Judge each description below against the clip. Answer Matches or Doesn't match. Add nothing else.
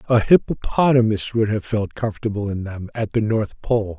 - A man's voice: Matches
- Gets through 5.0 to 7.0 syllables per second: Matches